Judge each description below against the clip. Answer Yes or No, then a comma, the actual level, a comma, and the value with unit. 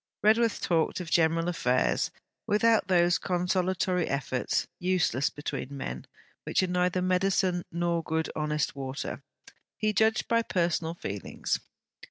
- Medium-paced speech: No, slow, 125 wpm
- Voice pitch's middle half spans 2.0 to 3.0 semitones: Yes, average, 2.7 semitones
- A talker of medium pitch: Yes, medium, 175 Hz